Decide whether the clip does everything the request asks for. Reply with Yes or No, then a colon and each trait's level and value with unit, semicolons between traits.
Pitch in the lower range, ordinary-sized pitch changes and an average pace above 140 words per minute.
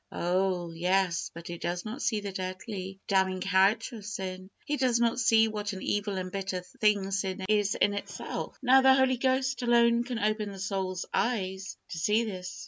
No: high, 200 Hz; average, 3.5 semitones; average, 190 wpm